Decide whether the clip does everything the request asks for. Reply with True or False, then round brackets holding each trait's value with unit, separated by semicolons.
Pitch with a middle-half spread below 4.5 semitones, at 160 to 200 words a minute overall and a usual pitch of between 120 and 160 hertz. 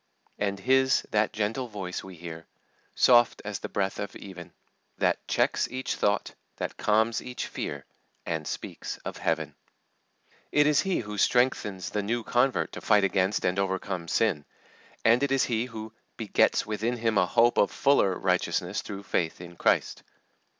False (4.0 semitones; 165 wpm; 105 Hz)